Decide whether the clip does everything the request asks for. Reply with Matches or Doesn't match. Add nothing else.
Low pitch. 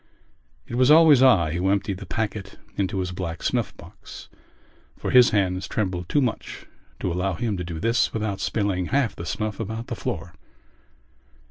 Matches